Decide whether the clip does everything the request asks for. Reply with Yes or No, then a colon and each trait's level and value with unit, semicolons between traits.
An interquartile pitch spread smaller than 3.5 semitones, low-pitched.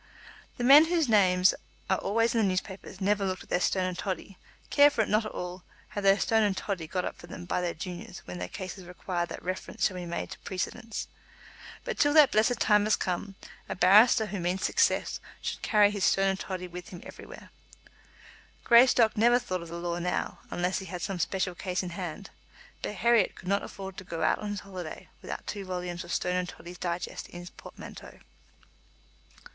No: average, 2.8 semitones; high, 190 Hz